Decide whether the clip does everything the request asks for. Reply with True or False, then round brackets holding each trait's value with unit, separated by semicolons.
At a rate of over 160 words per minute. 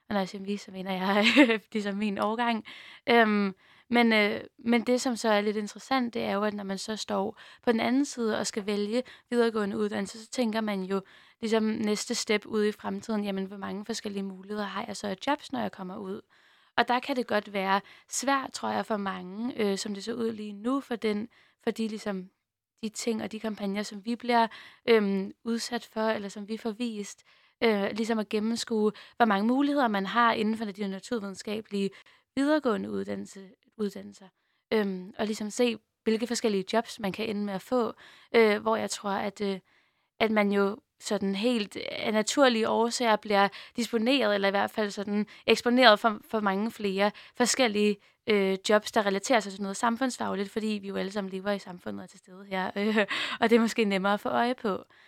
True (205 wpm)